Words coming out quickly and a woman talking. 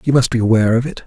No: fast, 340 wpm; male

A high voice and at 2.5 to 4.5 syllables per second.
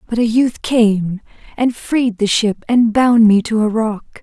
Yes: high, 225 Hz; 4.1 syllables/s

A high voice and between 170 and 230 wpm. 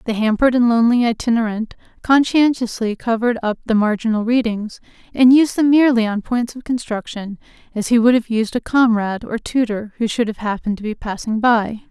Yes: high, 230 Hz; average, 180 wpm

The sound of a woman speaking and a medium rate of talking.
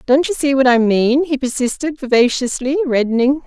Yes: female; average, 175 wpm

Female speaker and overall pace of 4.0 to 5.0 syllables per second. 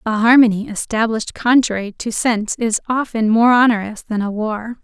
No: female; 5.3 syllables/s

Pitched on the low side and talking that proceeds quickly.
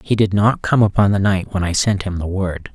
Yes: very low, 95 Hz; fast, 285 wpm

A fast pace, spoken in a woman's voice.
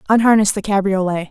No: average, 140 wpm; female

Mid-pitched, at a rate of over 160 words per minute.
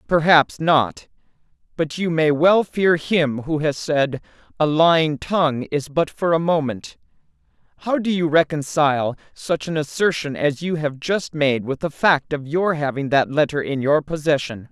Yes: medium, 155 Hz; average, 170 wpm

